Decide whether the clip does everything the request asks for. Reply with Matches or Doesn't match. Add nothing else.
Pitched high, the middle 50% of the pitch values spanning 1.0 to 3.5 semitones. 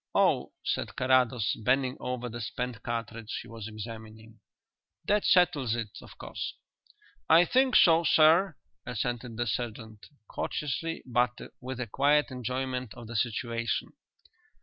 Doesn't match